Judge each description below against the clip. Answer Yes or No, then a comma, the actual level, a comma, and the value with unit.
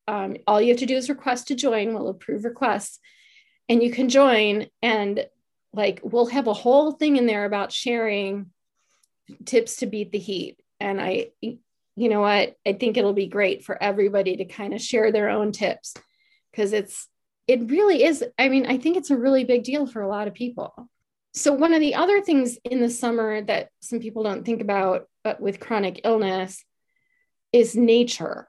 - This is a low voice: No, high, 235 Hz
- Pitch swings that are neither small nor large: Yes, average, 4.4 semitones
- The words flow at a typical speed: Yes, average, 195 wpm